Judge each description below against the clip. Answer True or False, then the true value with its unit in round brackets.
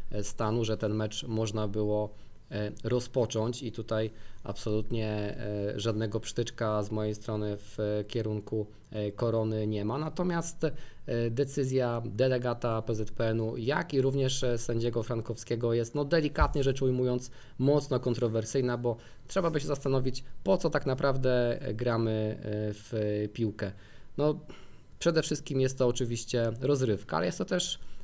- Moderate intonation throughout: True (3.4 semitones)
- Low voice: True (115 Hz)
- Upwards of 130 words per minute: False (125 wpm)